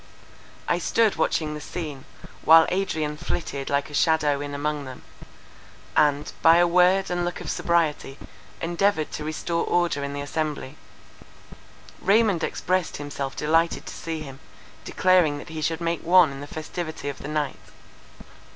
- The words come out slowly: No, average, 155 wpm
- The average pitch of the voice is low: No, medium, 155 Hz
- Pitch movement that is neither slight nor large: Yes, average, 3.0 semitones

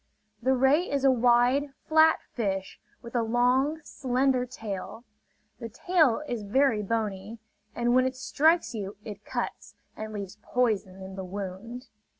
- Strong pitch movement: No, average, 4.1 semitones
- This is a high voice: Yes, high, 240 Hz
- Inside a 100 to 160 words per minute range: Yes, average, 150 wpm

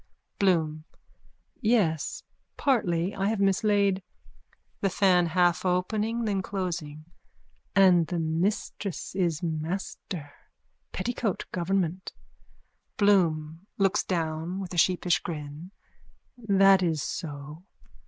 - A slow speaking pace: Yes, slow, 95 wpm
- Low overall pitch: No, medium, 180 Hz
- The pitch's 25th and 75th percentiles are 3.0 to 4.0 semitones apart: Yes, average, 3.4 semitones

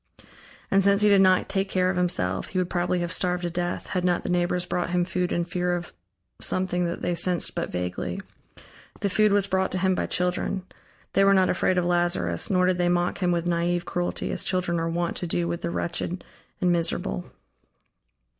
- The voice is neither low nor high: Yes, medium, 180 Hz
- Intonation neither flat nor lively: No, narrow, 1.2 semitones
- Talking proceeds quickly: Yes, fast, 210 wpm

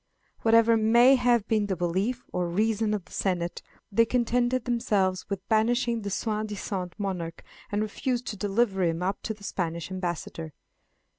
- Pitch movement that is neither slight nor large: Yes, average, 3.8 semitones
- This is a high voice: Yes, high, 210 Hz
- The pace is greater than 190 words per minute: No, average, 160 wpm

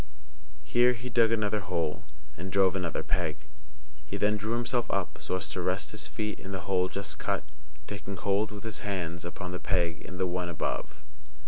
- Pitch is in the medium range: No, very low, 95 Hz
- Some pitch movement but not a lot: Yes, average, 3.0 semitones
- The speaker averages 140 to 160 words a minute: No, average, 195 wpm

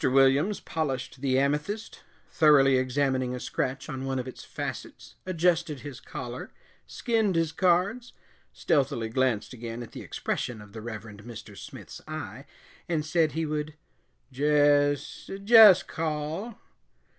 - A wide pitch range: No, average, 4.0 semitones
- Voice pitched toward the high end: No, medium, 145 Hz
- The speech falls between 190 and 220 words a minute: No, slow, 135 wpm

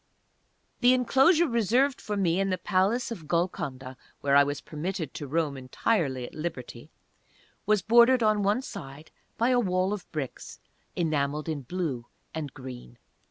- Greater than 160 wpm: No, average, 155 wpm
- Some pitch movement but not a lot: No, wide, 7.2 semitones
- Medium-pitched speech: Yes, medium, 175 Hz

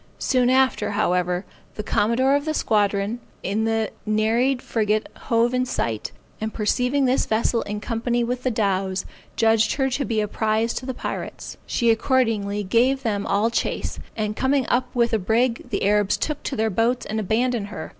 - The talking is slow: No, average, 180 wpm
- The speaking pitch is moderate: No, high, 225 Hz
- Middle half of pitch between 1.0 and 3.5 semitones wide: Yes, average, 3.0 semitones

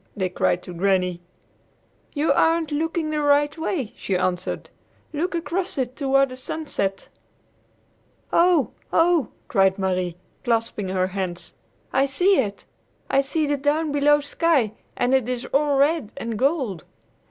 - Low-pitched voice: No, very high, 275 Hz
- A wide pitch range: Yes, wide, 7.6 semitones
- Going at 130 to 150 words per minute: Yes, average, 140 wpm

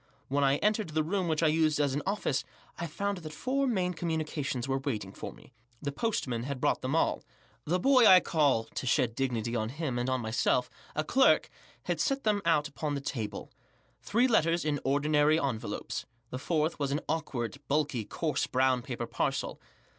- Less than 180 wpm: No, average, 185 wpm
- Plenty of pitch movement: No, average, 4.3 semitones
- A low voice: No, medium, 150 Hz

